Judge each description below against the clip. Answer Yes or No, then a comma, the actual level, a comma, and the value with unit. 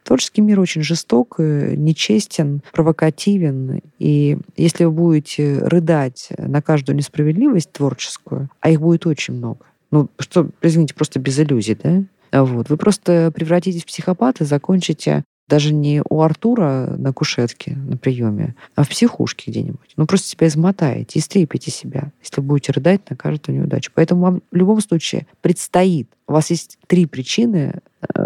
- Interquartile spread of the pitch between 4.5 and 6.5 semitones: No, average, 3.5 semitones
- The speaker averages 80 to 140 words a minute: No, average, 150 wpm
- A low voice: No, medium, 160 Hz